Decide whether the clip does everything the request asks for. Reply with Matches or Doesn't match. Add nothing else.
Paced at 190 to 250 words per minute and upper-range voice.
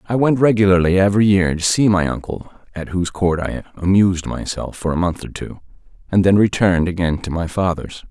Doesn't match